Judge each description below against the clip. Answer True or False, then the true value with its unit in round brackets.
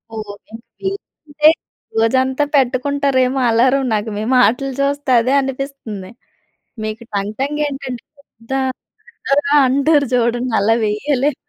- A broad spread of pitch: False (3.7 semitones)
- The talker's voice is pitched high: True (260 Hz)